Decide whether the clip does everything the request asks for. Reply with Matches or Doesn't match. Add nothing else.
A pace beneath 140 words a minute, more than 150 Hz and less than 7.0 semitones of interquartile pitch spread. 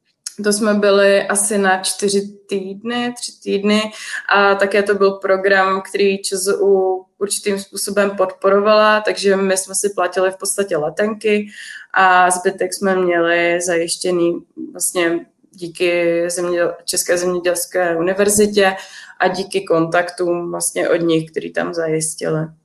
Matches